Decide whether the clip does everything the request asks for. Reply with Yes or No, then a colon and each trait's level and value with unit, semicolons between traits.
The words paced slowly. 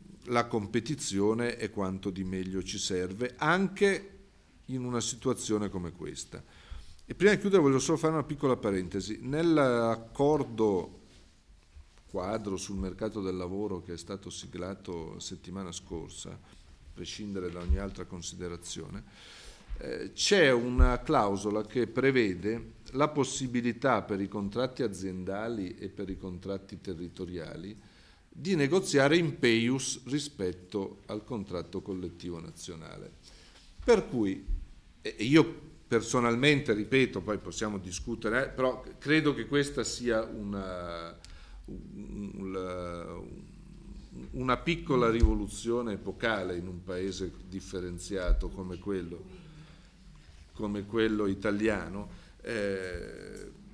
Yes: slow, 110 wpm